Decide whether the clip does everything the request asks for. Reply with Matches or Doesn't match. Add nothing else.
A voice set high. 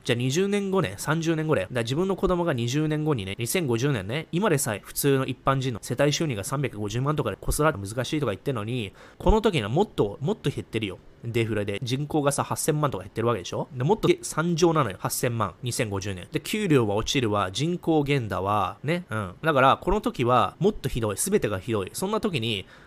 Doesn't match